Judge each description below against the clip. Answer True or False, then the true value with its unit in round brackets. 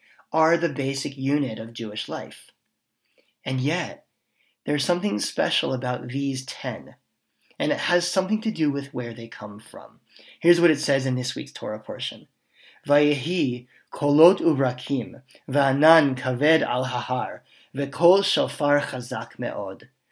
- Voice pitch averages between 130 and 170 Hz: True (140 Hz)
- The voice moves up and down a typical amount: True (4.1 semitones)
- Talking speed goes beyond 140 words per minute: False (135 wpm)